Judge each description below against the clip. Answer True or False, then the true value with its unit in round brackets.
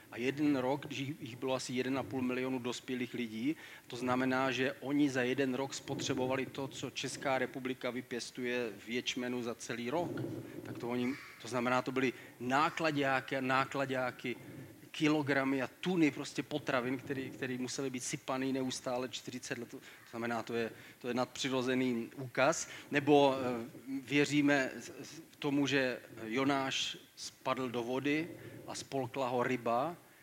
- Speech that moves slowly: False (140 wpm)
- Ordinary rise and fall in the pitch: False (2.0 semitones)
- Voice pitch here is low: True (130 Hz)